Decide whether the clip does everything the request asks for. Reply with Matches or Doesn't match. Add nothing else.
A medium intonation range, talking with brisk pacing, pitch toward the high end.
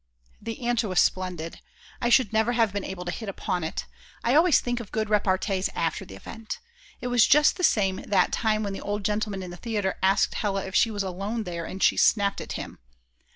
Matches